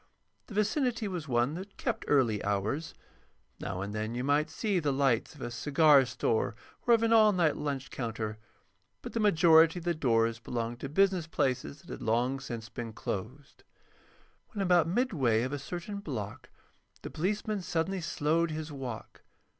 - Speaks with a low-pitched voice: No, medium, 145 Hz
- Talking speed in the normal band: Yes, average, 170 wpm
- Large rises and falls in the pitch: Yes, wide, 6.9 semitones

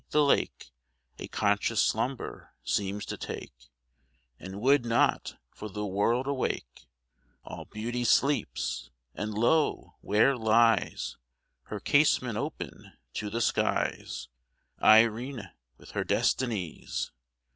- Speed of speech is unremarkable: No, slow, 110 wpm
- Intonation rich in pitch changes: No, average, 3.6 semitones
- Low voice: Yes, low, 110 Hz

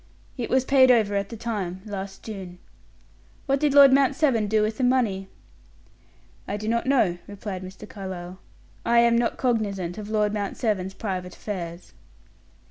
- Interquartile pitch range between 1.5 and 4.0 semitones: Yes, average, 3.7 semitones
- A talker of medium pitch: No, high, 210 Hz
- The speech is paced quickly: No, average, 165 wpm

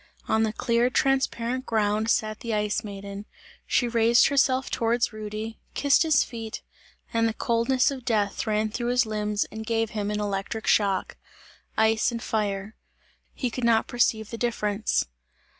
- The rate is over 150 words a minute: Yes, average, 160 wpm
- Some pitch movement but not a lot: No, narrow, 2.1 semitones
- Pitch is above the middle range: Yes, high, 225 Hz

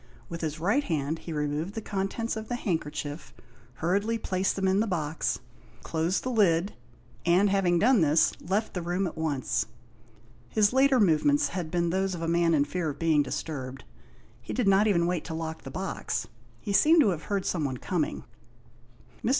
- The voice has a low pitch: No, medium, 175 Hz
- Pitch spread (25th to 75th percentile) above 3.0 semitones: Yes, average, 4.1 semitones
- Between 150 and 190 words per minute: Yes, average, 185 wpm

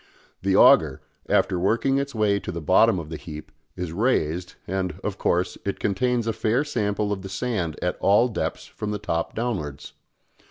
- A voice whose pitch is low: Yes, low, 100 Hz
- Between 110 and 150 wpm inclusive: No, average, 185 wpm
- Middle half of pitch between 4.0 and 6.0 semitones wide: Yes, average, 4.3 semitones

